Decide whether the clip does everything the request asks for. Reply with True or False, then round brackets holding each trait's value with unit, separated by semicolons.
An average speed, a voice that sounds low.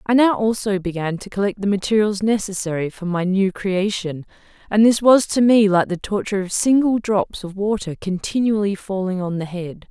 False (190 wpm; 200 Hz)